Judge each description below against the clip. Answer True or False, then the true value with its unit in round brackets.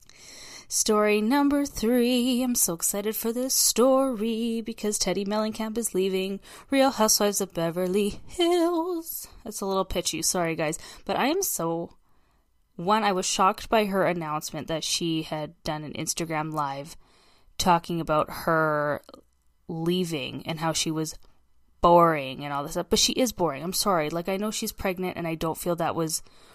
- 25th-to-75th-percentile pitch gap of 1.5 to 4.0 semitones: False (5.5 semitones)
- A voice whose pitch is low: False (180 Hz)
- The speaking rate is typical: True (165 wpm)